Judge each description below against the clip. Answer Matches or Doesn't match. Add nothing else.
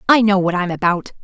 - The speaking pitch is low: Doesn't match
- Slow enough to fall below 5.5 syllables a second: Doesn't match